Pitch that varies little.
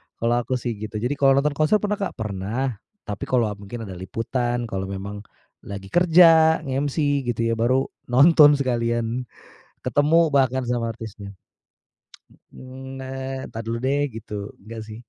No: average, 3.5 semitones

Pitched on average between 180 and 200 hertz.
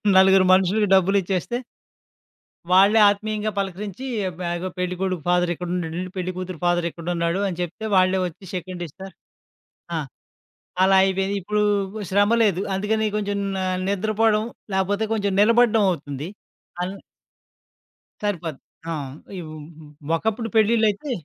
Yes: high, 190 Hz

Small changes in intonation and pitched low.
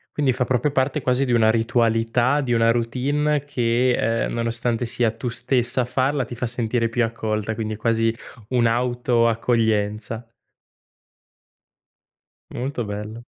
Yes: narrow, 1.8 semitones; low, 120 Hz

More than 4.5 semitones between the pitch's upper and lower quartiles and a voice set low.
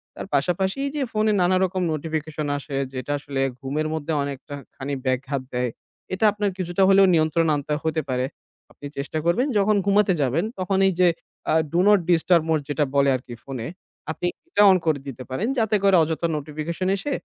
No: average, 5.0 semitones; medium, 160 Hz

